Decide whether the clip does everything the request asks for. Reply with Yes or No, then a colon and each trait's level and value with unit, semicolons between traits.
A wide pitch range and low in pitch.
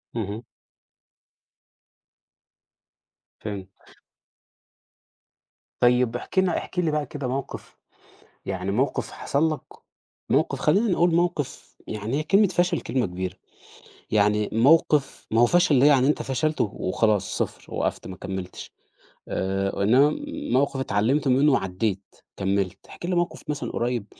Yes: wide, 6.8 semitones; low, 125 Hz